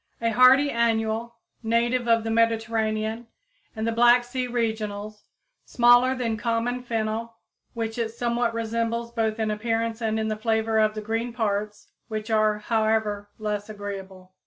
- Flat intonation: Yes, narrow, 1.4 semitones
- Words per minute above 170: No, average, 150 wpm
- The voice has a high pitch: Yes, high, 225 Hz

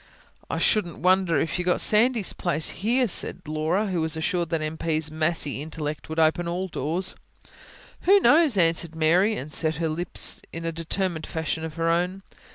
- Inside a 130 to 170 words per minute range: No, average, 180 wpm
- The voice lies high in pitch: No, medium, 165 Hz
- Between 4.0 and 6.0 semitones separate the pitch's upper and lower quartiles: No, average, 2.7 semitones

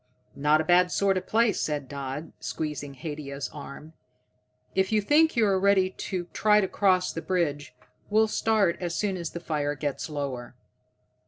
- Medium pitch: Yes, medium, 170 Hz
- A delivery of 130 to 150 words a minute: No, average, 165 wpm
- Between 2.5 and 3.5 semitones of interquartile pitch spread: No, average, 5.1 semitones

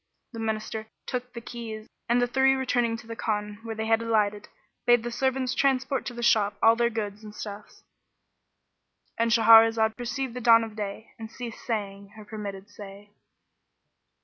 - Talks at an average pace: Yes, average, 170 wpm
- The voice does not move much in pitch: Yes, narrow, 2.2 semitones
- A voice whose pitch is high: Yes, high, 225 Hz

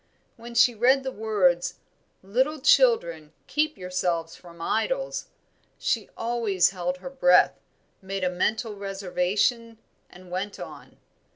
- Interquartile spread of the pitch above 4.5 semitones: Yes, average, 5.0 semitones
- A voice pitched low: No, high, 200 Hz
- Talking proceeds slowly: Yes, slow, 120 wpm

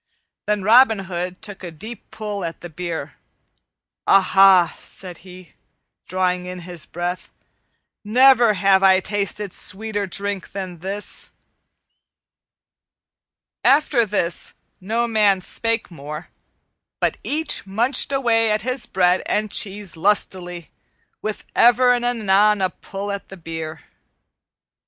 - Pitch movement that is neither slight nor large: Yes, average, 3.2 semitones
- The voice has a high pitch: Yes, high, 195 Hz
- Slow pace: Yes, slow, 120 wpm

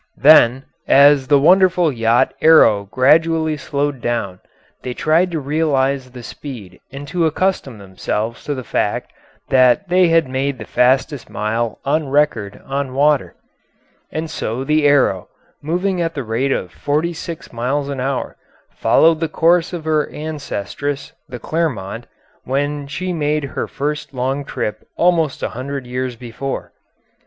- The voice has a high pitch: No, medium, 140 Hz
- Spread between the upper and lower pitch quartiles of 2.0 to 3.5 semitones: No, average, 4.0 semitones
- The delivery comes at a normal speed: Yes, average, 145 wpm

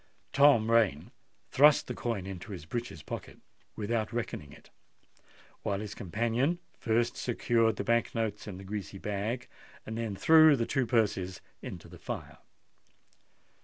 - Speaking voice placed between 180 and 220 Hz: No, low, 110 Hz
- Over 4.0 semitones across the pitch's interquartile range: No, average, 3.1 semitones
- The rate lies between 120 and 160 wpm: Yes, average, 145 wpm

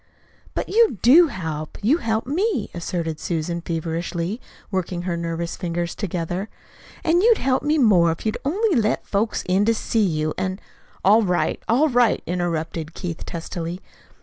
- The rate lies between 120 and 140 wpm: No, average, 160 wpm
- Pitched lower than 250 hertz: Yes, medium, 185 Hz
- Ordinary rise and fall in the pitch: No, wide, 5.9 semitones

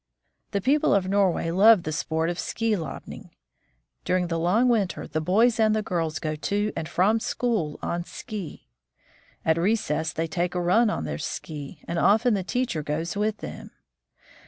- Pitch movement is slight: No, average, 4.9 semitones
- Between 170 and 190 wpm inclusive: Yes, average, 175 wpm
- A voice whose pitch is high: No, medium, 180 Hz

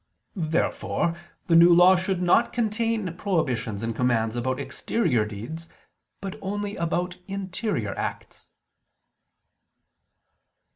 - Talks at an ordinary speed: No, slow, 100 wpm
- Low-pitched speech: No, medium, 175 Hz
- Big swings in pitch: Yes, wide, 7.8 semitones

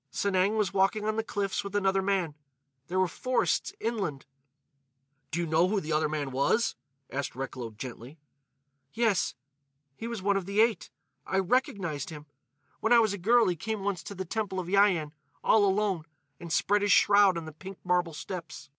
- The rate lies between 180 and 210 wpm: Yes, average, 185 wpm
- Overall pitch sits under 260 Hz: Yes, high, 190 Hz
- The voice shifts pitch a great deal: No, average, 3.9 semitones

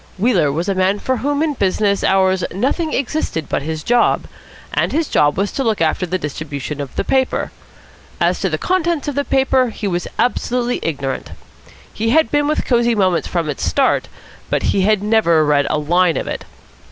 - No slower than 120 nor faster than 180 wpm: No, average, 195 wpm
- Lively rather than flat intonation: Yes, wide, 7.9 semitones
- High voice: Yes, high, 200 Hz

